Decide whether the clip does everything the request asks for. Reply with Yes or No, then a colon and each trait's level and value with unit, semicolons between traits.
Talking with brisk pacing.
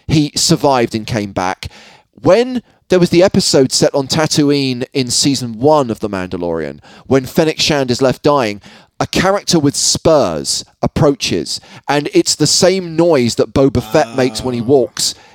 No: average, 165 wpm